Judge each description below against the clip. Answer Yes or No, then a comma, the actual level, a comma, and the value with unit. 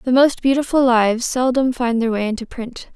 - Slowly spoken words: No, fast, 205 wpm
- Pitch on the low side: No, high, 245 Hz